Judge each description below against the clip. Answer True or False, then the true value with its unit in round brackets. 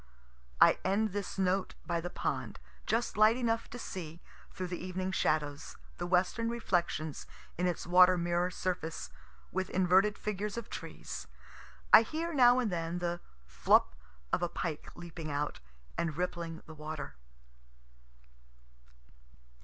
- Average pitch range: True (3.4 semitones)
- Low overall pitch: False (180 Hz)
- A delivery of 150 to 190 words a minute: False (135 wpm)